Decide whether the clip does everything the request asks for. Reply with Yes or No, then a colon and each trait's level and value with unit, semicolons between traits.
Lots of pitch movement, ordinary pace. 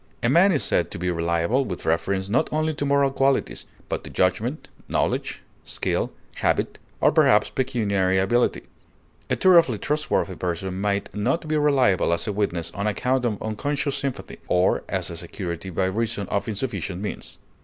Yes: wide, 6.4 semitones; average, 165 wpm